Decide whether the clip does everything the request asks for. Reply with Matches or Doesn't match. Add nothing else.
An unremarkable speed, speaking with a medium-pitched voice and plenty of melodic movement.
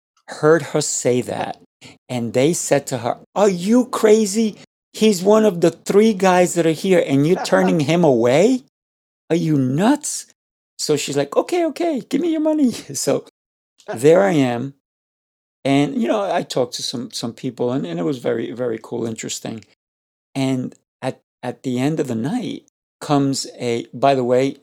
Matches